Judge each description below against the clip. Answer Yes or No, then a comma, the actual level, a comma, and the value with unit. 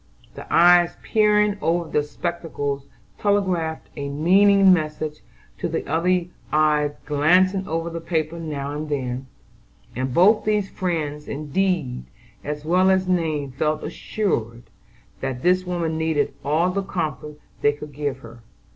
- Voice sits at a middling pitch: Yes, medium, 160 Hz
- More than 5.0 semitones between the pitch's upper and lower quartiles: No, average, 3.8 semitones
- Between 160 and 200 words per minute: No, average, 140 wpm